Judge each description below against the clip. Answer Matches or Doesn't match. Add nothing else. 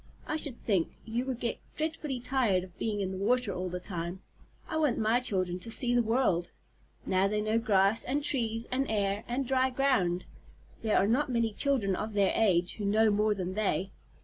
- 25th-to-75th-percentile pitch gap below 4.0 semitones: Doesn't match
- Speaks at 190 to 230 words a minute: Matches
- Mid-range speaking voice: Doesn't match